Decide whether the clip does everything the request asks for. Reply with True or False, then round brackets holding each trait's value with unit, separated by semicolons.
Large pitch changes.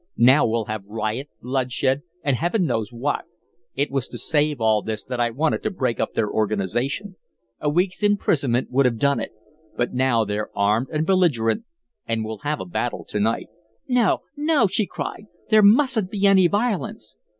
True (8.5 semitones)